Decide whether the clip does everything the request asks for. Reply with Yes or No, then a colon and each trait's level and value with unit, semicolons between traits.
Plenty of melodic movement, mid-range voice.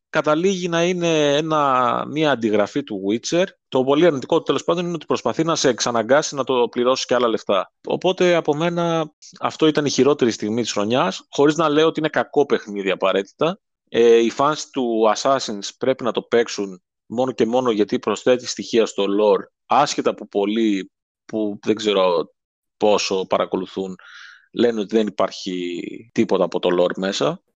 No: wide, 6.9 semitones; low, 125 Hz